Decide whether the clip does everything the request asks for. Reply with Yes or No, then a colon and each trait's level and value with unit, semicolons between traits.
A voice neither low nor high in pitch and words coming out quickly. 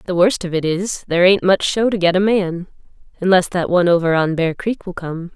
Yes: medium, 180 Hz; fast, 245 wpm